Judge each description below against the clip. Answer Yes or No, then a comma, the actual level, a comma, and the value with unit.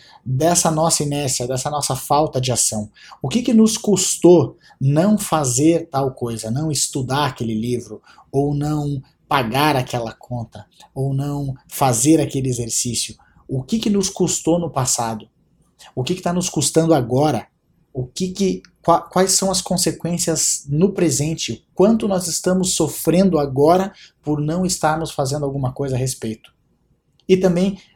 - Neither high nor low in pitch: Yes, medium, 150 Hz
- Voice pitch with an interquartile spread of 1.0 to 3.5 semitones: No, average, 5.1 semitones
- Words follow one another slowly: No, average, 145 wpm